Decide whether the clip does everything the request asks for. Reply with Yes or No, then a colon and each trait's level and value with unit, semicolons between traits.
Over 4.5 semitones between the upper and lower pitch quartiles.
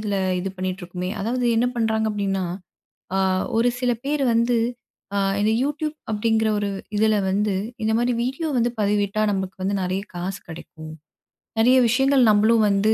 No: average, 3.6 semitones